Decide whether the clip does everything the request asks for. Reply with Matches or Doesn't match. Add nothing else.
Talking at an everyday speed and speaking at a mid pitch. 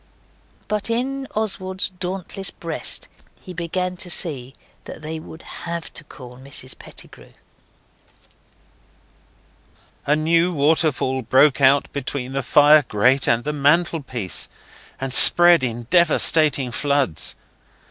Doesn't match